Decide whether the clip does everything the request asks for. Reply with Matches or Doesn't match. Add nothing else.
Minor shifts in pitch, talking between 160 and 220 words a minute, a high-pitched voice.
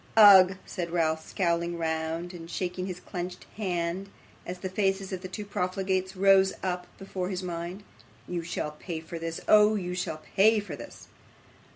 Doesn't match